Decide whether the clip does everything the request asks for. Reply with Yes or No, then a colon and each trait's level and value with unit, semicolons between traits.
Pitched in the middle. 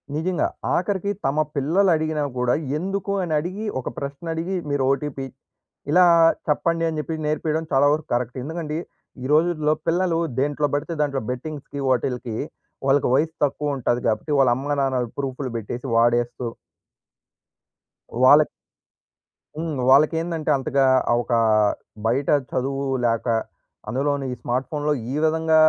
Yes: medium, 145 Hz